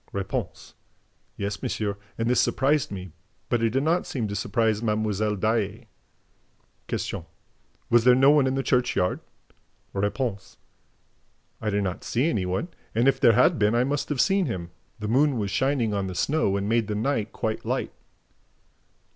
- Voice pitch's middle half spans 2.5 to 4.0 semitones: No, average, 4.4 semitones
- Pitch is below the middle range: Yes, low, 115 Hz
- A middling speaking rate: Yes, average, 165 wpm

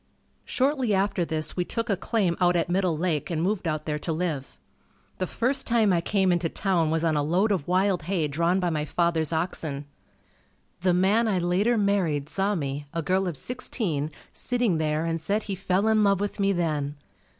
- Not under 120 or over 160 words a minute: No, average, 200 wpm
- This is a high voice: No, medium, 180 Hz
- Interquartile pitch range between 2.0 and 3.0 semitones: No, average, 3.9 semitones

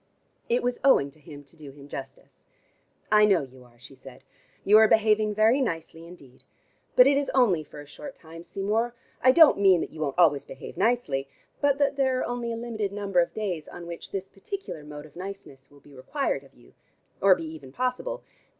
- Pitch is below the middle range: No, high, 190 Hz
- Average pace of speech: No, fast, 210 wpm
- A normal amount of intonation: No, wide, 8.3 semitones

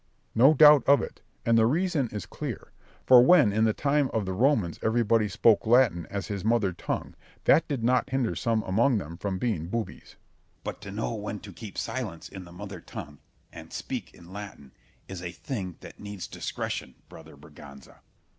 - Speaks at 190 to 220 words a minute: Yes, average, 195 wpm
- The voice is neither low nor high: No, low, 110 Hz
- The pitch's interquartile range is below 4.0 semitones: No, average, 5.1 semitones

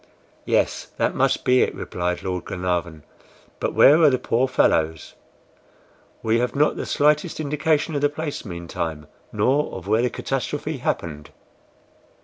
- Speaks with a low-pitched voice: Yes, low, 125 Hz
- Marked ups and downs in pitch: Yes, wide, 8.8 semitones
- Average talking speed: Yes, average, 150 wpm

